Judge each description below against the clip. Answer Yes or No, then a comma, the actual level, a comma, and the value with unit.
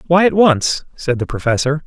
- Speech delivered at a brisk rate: No, average, 195 wpm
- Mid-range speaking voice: Yes, medium, 150 Hz